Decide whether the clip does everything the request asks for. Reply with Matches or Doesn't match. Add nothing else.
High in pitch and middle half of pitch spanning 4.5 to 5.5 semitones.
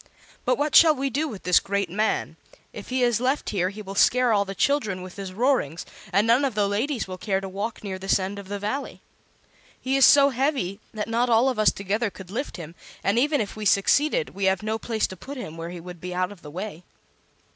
Matches